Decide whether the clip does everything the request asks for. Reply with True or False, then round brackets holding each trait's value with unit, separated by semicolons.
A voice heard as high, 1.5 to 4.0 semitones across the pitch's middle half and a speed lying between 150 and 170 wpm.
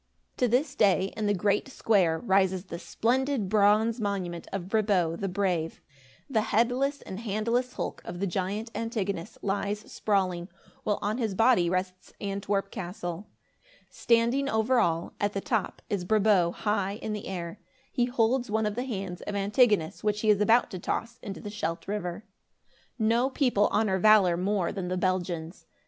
True (205 Hz; 3.3 semitones; 165 wpm)